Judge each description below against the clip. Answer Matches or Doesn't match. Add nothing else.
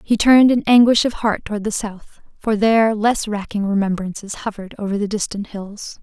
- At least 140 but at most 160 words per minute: Doesn't match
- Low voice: Doesn't match